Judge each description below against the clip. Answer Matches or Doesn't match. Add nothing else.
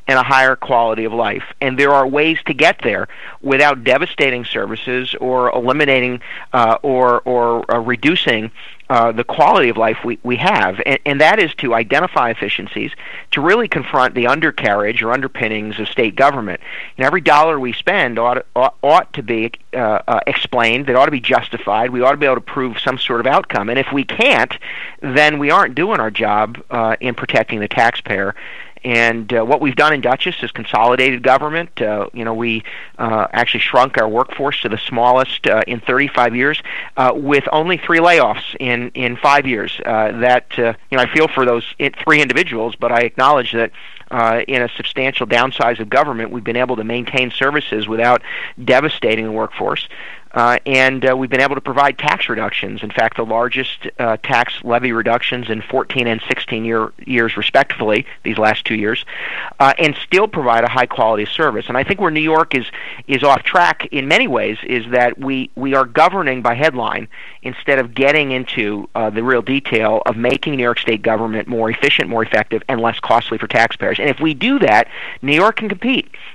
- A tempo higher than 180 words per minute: Matches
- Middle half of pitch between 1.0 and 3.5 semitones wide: Matches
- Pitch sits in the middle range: Doesn't match